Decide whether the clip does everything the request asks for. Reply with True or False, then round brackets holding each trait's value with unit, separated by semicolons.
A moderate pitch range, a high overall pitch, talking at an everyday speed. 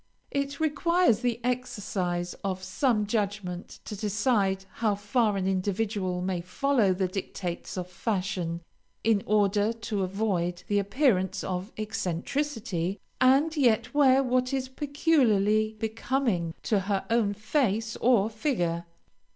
False (4.9 semitones; 210 Hz; 125 wpm)